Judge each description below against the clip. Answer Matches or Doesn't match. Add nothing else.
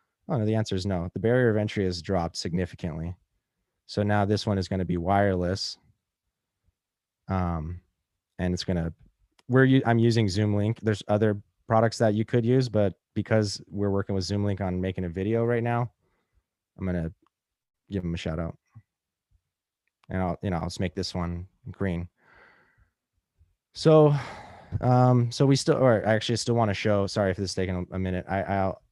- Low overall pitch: Matches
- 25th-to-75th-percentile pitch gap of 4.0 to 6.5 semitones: Doesn't match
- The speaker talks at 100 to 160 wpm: Doesn't match